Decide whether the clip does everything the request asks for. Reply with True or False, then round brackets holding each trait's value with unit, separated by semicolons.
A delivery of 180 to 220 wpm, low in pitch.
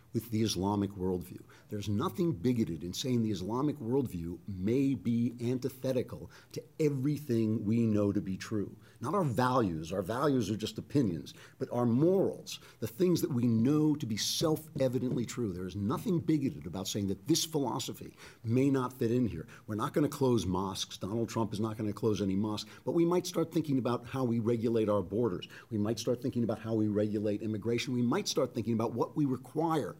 True (200 wpm; 120 Hz)